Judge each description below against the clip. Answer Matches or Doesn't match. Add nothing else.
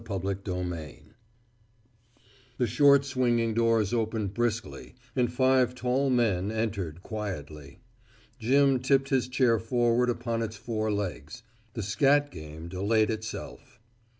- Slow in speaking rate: Matches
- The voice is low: Matches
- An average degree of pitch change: Matches